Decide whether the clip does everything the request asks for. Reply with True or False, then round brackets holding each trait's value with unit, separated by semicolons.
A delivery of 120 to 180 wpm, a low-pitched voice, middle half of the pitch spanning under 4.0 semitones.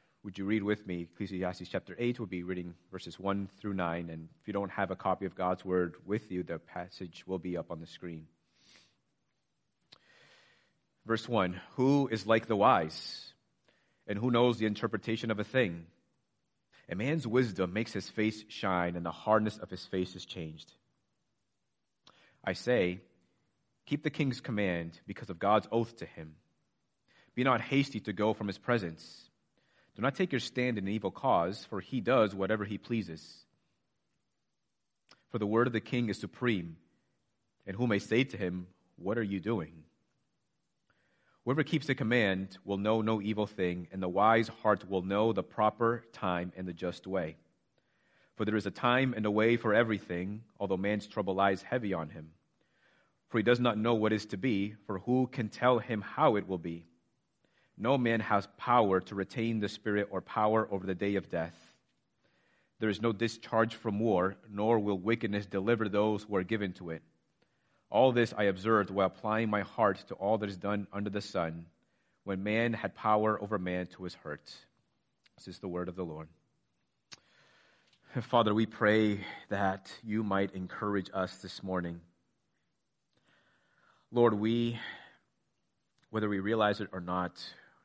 True (175 wpm; 100 Hz; 3.6 semitones)